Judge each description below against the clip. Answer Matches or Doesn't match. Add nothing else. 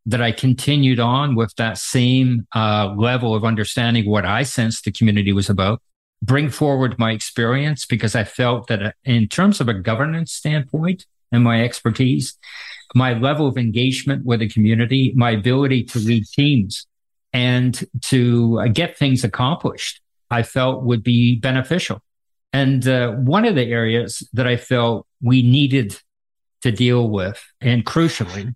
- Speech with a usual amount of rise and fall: Doesn't match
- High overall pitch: Doesn't match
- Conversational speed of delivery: Matches